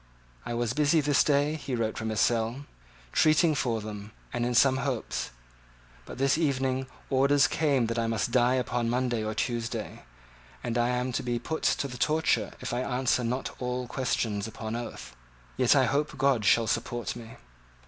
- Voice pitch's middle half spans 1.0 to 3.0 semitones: Yes, average, 2.7 semitones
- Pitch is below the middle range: Yes, low, 125 Hz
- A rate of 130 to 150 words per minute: No, average, 180 wpm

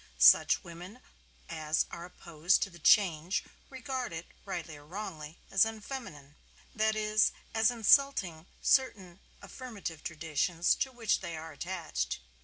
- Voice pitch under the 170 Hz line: No, medium, 180 Hz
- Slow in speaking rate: Yes, slow, 130 wpm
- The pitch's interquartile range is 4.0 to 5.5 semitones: Yes, average, 5.2 semitones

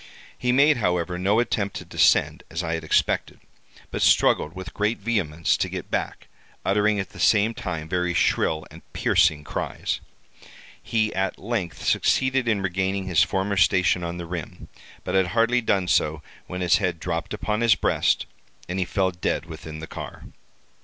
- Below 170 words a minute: No, average, 175 wpm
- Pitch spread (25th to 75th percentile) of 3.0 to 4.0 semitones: Yes, average, 3.7 semitones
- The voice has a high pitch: No, very low, 95 Hz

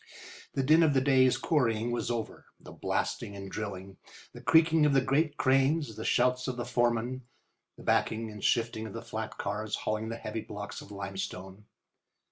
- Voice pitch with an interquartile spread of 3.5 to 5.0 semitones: Yes, average, 3.8 semitones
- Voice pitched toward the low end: Yes, low, 115 Hz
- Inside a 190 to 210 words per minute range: No, average, 175 wpm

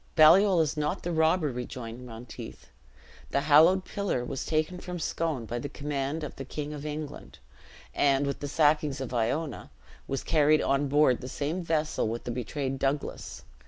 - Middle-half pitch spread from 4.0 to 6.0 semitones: No, average, 3.0 semitones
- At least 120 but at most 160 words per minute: No, average, 170 wpm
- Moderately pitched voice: Yes, medium, 145 Hz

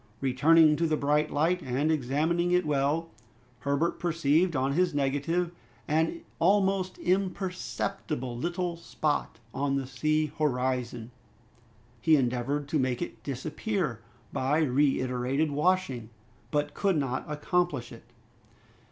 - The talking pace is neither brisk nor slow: No, slow, 115 wpm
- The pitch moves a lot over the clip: No, average, 4.0 semitones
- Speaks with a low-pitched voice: No, medium, 150 Hz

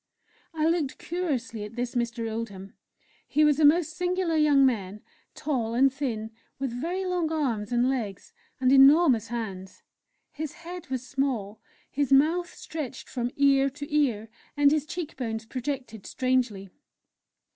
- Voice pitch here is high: Yes, very high, 270 Hz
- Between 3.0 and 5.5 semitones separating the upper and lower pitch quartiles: Yes, average, 4.8 semitones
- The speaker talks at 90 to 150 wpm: Yes, average, 145 wpm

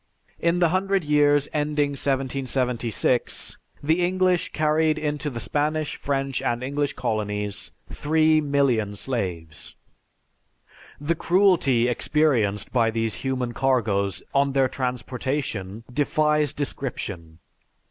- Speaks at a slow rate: Yes, slow, 105 wpm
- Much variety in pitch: No, average, 4.4 semitones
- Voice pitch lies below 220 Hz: Yes, low, 135 Hz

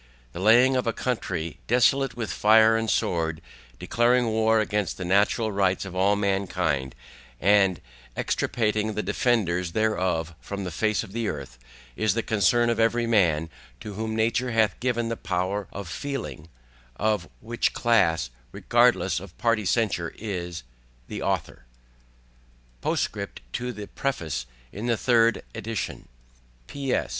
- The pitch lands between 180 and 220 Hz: No, low, 105 Hz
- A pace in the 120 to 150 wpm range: Yes, average, 140 wpm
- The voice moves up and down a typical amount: Yes, average, 4.1 semitones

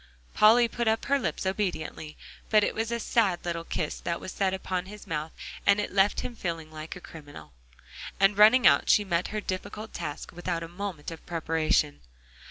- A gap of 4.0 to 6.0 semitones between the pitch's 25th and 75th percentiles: Yes, average, 4.3 semitones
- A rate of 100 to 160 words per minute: No, average, 190 wpm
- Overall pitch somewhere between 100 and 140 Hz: No, medium, 185 Hz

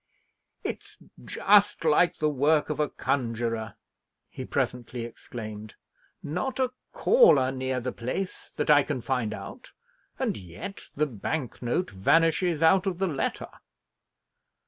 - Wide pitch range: Yes, wide, 6.1 semitones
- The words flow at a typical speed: No, slow, 130 wpm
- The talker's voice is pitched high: No, medium, 145 Hz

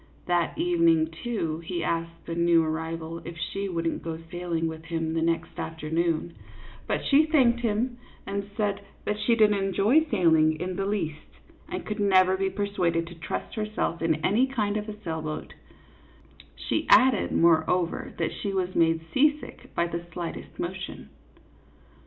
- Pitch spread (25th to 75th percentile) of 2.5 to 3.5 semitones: No, average, 4.2 semitones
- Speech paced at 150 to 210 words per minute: Yes, average, 160 wpm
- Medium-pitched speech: Yes, medium, 180 Hz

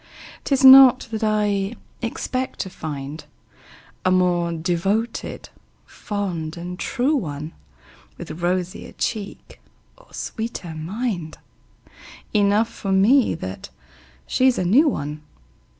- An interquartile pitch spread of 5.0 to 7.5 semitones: Yes, average, 5.3 semitones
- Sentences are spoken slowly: Yes, slow, 105 wpm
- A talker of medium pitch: No, high, 195 Hz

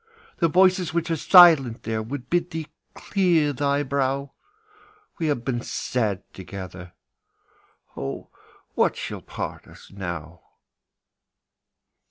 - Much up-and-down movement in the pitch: Yes, wide, 7.2 semitones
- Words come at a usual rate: No, slow, 115 wpm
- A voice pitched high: No, medium, 140 Hz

